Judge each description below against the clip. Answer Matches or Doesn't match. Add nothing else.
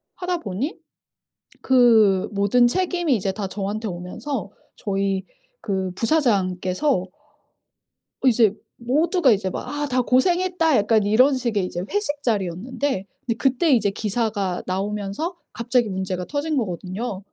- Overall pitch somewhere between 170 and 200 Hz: Doesn't match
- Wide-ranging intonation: Matches